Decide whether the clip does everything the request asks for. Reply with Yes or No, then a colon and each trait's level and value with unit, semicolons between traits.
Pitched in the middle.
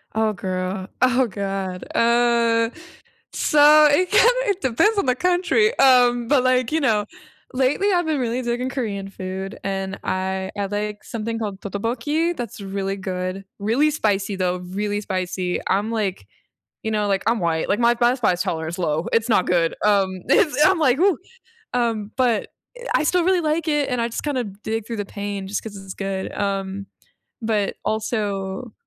No: high, 220 Hz